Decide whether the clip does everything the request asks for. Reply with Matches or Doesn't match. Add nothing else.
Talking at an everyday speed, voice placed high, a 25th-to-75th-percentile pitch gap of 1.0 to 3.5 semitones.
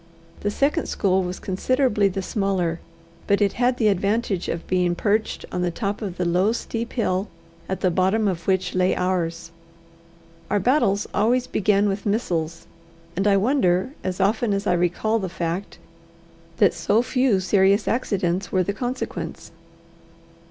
Matches